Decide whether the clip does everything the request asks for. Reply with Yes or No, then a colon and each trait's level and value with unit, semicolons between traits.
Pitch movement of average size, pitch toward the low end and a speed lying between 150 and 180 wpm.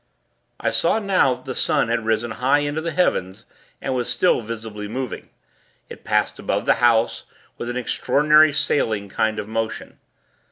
Yes: average, 4.6 semitones; low, 120 Hz; average, 165 wpm